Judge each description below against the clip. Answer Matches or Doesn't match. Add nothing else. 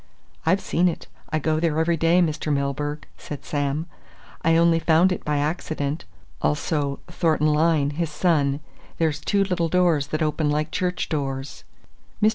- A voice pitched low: Doesn't match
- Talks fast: Doesn't match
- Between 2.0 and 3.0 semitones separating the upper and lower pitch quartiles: Matches